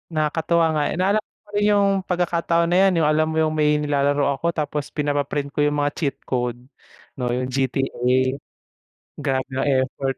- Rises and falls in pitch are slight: No, average, 3.2 semitones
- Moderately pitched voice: Yes, medium, 150 Hz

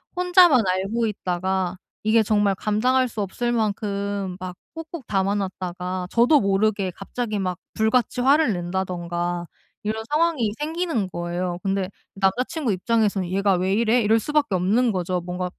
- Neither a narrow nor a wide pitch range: Yes, average, 4.2 semitones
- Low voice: No, high, 200 Hz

